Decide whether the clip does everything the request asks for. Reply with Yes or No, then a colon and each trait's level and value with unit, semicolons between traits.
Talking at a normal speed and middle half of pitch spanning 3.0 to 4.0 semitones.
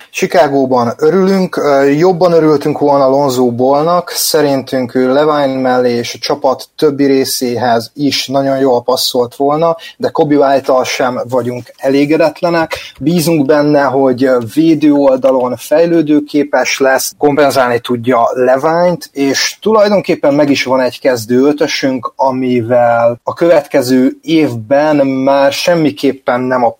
Yes: average, 120 wpm; average, 3.3 semitones